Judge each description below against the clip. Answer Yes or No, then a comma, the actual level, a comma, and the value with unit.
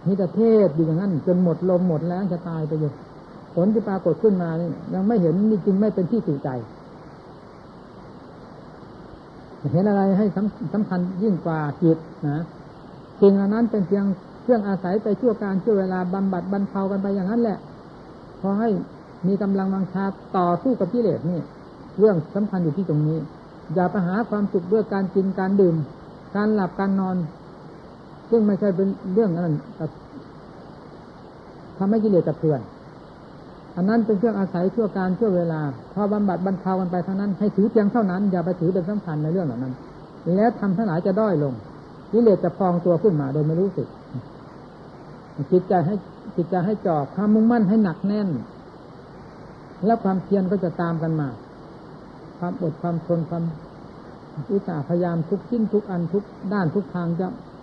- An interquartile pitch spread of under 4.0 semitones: Yes, average, 3.3 semitones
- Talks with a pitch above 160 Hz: Yes, high, 190 Hz